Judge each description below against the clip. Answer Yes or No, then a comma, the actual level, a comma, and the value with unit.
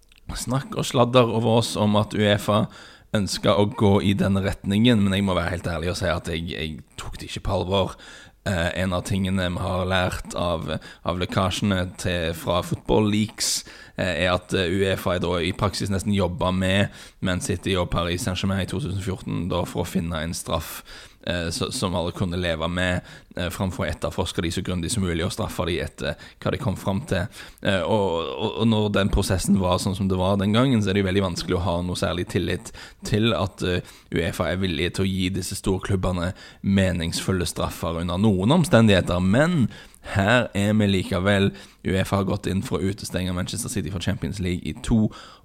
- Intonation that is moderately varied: No, narrow, 2.3 semitones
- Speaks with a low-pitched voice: Yes, very low, 95 Hz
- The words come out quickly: No, average, 190 wpm